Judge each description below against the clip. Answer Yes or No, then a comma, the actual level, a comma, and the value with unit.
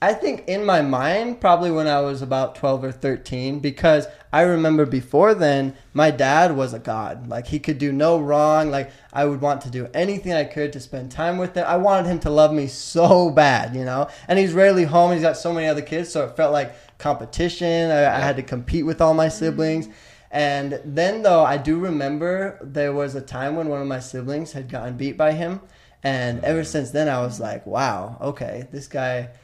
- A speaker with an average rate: No, fast, 220 wpm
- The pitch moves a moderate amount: Yes, average, 3.3 semitones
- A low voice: No, medium, 150 Hz